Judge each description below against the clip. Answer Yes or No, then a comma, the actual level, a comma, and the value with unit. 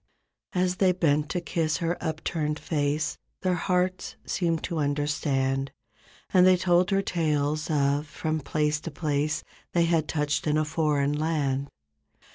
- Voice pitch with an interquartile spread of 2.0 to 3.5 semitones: Yes, average, 2.9 semitones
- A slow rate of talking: No, average, 145 wpm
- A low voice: No, medium, 155 Hz